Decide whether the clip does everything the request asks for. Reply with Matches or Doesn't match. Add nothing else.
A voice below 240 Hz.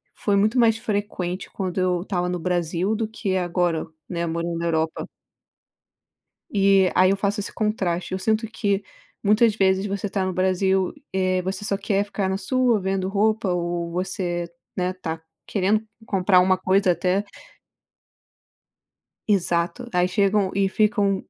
Matches